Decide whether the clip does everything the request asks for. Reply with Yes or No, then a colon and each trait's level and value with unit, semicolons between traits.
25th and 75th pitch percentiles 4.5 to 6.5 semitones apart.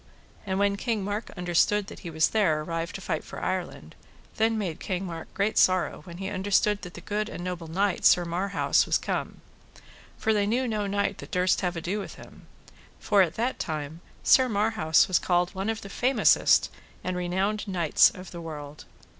No: average, 3.2 semitones